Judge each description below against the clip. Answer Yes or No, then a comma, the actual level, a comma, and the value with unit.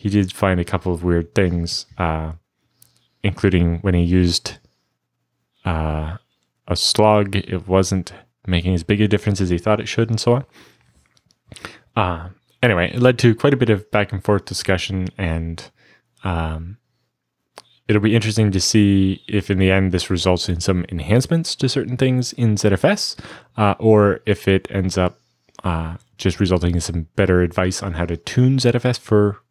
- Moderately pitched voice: No, very low, 95 Hz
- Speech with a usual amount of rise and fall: Yes, average, 3.3 semitones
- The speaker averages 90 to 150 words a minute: No, average, 170 wpm